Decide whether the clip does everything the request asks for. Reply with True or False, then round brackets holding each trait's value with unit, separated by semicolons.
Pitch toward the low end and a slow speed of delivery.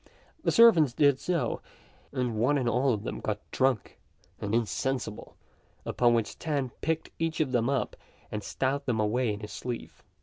False (125 Hz; 170 wpm)